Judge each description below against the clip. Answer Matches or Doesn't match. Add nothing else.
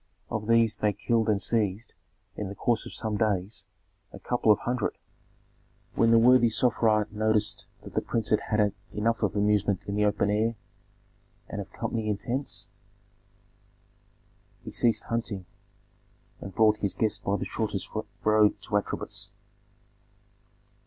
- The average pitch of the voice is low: Matches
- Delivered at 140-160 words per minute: Matches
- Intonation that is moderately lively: Doesn't match